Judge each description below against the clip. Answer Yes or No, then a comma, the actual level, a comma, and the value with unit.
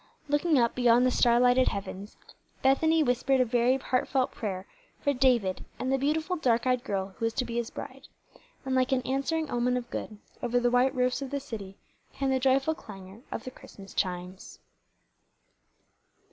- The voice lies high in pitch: Yes, very high, 250 Hz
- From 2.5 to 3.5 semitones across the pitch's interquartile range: Yes, average, 2.8 semitones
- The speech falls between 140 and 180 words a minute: Yes, average, 175 wpm